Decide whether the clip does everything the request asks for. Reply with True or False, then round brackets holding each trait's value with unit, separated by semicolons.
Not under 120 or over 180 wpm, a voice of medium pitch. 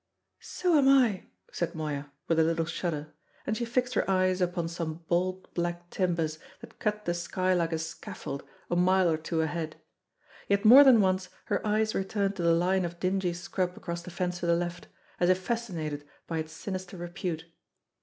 False (190 wpm; 175 Hz)